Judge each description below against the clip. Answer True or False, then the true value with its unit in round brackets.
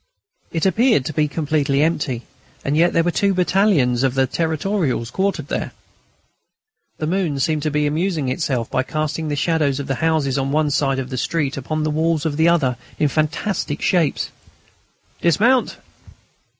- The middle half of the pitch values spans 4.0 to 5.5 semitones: False (3.3 semitones)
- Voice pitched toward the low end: False (155 Hz)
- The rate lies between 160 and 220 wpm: True (175 wpm)